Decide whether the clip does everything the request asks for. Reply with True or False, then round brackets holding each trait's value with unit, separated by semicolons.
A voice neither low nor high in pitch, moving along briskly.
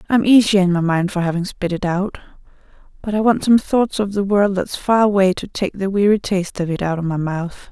False (195 Hz; 250 wpm)